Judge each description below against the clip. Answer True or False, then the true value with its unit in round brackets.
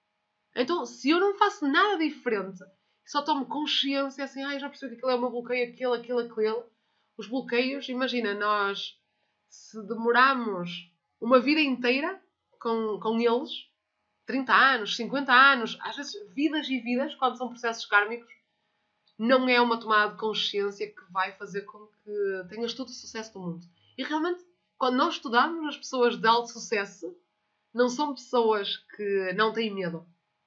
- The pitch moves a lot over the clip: False (4.5 semitones)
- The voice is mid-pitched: False (240 Hz)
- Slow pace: False (160 wpm)